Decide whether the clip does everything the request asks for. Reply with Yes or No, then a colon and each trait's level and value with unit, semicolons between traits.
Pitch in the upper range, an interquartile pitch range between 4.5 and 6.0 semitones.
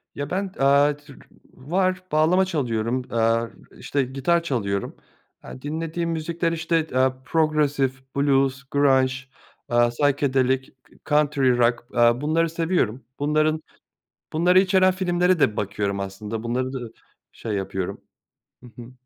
No: medium, 140 Hz; average, 5.0 semitones